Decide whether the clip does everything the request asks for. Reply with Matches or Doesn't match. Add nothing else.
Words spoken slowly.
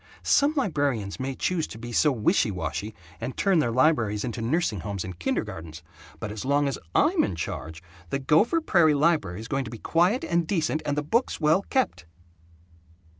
Doesn't match